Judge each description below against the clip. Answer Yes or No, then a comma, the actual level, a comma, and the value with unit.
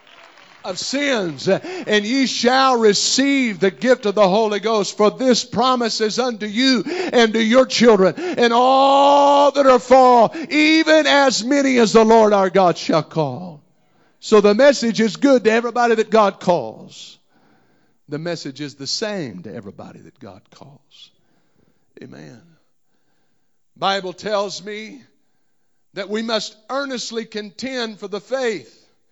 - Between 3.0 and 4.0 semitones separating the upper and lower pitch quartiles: No, average, 4.4 semitones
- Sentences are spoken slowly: No, average, 145 wpm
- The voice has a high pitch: Yes, high, 225 Hz